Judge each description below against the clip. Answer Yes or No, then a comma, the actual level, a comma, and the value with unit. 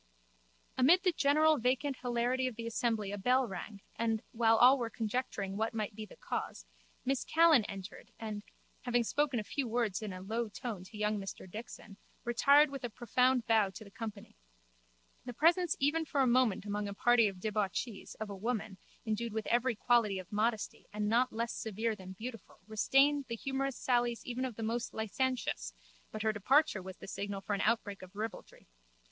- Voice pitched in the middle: No, high, 230 Hz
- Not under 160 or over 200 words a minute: Yes, average, 190 wpm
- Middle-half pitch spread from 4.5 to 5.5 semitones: No, average, 3.4 semitones